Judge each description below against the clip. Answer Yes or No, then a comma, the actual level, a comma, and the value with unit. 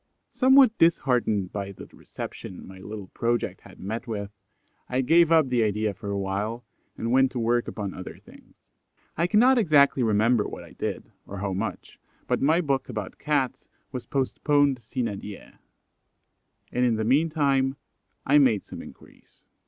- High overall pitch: No, low, 120 Hz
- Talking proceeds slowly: No, average, 160 wpm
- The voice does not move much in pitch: No, wide, 5.4 semitones